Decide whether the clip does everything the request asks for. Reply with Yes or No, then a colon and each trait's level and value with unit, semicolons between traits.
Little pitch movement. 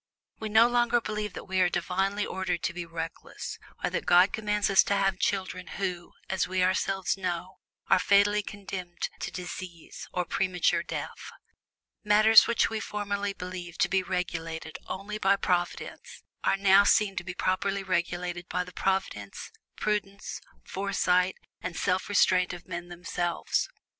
Yes: narrow, 2.1 semitones